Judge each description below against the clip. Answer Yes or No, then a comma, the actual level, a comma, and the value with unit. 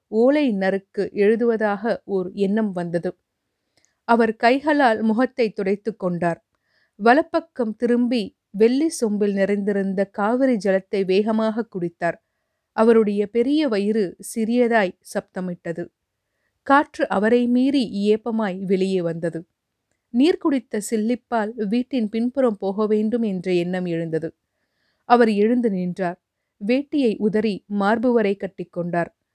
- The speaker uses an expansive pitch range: No, average, 3.7 semitones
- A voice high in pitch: Yes, high, 215 Hz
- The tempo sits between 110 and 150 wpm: No, average, 100 wpm